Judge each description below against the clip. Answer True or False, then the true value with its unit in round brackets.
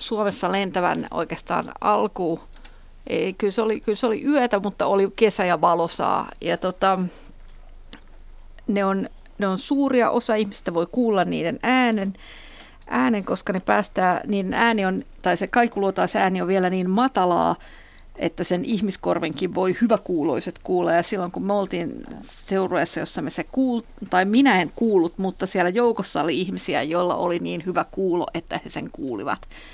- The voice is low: False (195 Hz)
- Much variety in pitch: False (3.5 semitones)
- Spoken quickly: True (160 wpm)